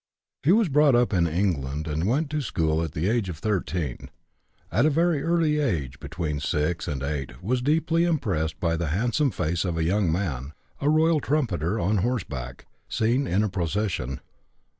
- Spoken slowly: No, average, 180 wpm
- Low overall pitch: Yes, very low, 95 Hz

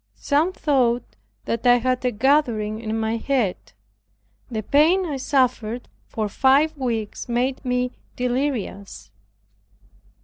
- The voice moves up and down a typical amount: Yes, average, 3.6 semitones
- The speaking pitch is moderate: No, very high, 250 Hz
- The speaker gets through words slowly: Yes, slow, 115 wpm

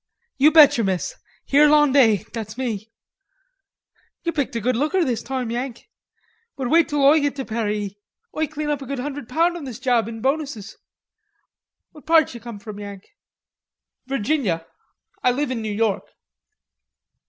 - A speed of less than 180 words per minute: Yes, average, 160 wpm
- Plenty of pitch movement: No, average, 4.8 semitones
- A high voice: Yes, very high, 255 Hz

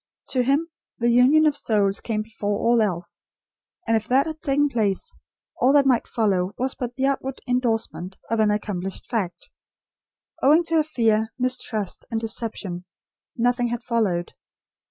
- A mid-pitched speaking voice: No, high, 235 Hz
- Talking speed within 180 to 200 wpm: No, average, 155 wpm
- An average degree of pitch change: Yes, average, 3.9 semitones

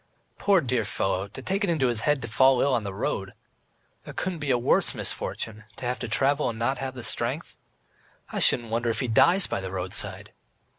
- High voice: No, low, 125 Hz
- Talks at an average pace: No, fast, 215 wpm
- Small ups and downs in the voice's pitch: No, average, 3.6 semitones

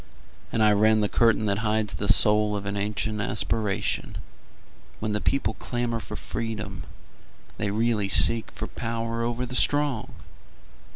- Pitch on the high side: No, low, 110 Hz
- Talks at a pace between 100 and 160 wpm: Yes, average, 150 wpm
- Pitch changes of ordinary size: No, narrow, 1.7 semitones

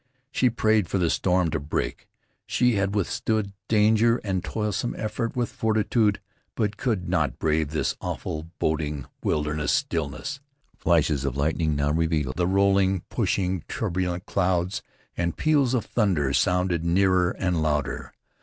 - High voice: No, very low, 90 Hz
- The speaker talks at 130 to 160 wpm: Yes, average, 140 wpm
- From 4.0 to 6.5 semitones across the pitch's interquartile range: Yes, average, 5.1 semitones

